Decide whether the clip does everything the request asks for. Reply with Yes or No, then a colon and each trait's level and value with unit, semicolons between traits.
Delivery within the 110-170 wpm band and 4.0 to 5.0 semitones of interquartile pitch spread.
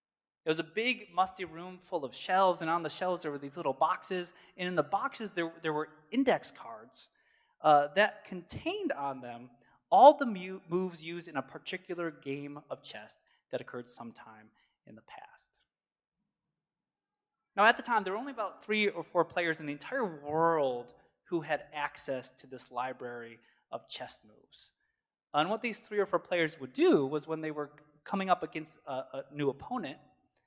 No: average, 185 wpm; average, 4.4 semitones